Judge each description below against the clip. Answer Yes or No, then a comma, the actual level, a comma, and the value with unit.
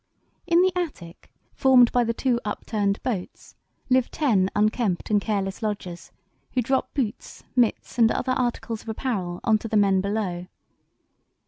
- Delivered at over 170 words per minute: No, average, 150 wpm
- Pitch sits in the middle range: No, high, 220 Hz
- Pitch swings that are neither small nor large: Yes, average, 4.0 semitones